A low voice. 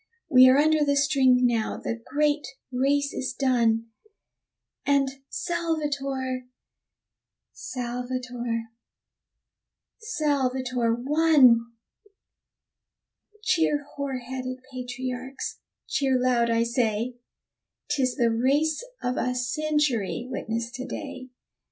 No: very high, 255 Hz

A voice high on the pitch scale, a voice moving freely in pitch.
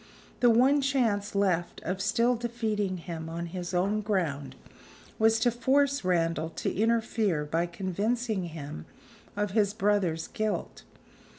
No: high, 200 Hz; average, 4.7 semitones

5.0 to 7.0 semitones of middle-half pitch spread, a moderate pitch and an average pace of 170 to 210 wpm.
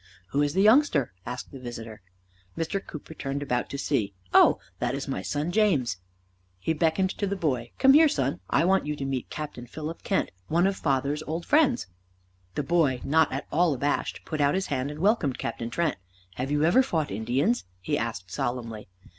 Yes: average, 5.3 semitones; medium, 145 Hz; average, 190 wpm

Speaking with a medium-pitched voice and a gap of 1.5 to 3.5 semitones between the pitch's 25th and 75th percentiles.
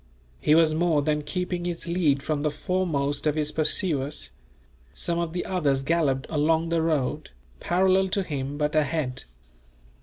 Yes: medium, 155 Hz; average, 2.9 semitones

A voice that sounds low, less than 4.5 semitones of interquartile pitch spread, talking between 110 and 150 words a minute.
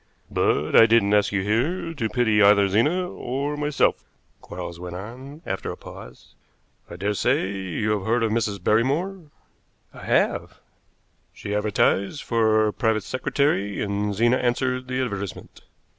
Yes: low, 110 Hz; average, 4.1 semitones; average, 145 wpm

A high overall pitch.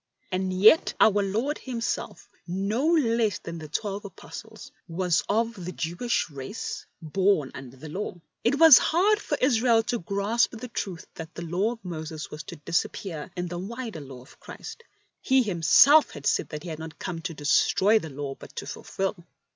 Yes: high, 195 Hz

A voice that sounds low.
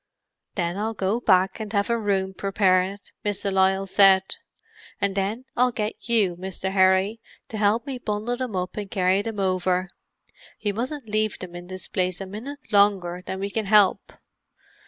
No: high, 200 Hz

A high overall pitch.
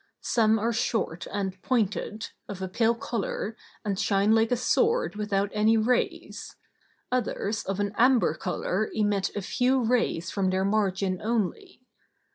Yes: high, 215 Hz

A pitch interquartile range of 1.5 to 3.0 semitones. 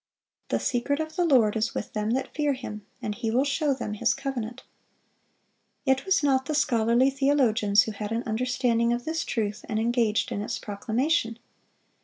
No: average, 3.8 semitones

